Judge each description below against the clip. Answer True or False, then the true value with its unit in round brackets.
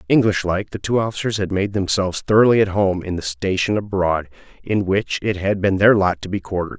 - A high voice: False (95 Hz)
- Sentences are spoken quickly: True (220 wpm)